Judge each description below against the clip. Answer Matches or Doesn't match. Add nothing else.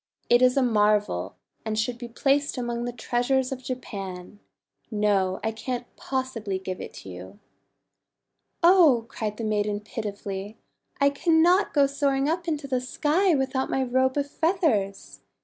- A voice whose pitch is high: Matches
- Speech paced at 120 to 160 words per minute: Matches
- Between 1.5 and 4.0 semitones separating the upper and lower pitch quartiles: Doesn't match